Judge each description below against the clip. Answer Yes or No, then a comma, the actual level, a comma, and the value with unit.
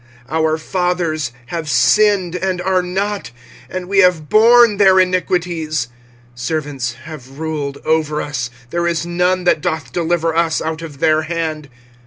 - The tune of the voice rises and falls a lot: No, average, 2.7 semitones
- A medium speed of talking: Yes, average, 155 wpm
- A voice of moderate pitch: Yes, medium, 165 Hz